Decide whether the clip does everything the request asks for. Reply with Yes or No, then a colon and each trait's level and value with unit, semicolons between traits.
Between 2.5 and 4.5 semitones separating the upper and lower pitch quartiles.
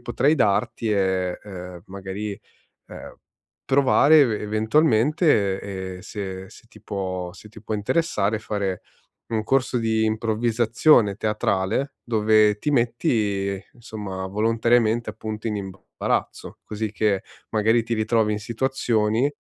Yes: average, 2.9 semitones